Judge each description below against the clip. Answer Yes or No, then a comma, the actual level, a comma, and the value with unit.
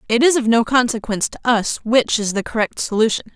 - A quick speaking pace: Yes, fast, 215 wpm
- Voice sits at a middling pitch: No, high, 230 Hz